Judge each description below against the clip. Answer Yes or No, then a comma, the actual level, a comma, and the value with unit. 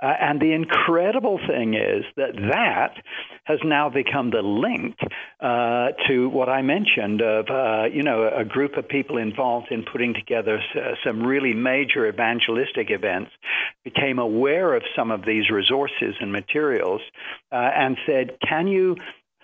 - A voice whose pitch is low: Yes, low, 130 Hz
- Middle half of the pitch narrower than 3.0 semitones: No, average, 5.0 semitones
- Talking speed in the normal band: Yes, average, 155 wpm